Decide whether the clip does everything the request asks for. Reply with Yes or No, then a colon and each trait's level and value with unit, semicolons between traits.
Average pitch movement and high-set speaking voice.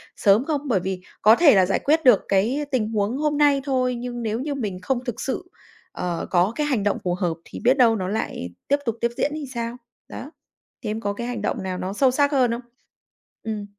Yes: average, 5.0 semitones; high, 235 Hz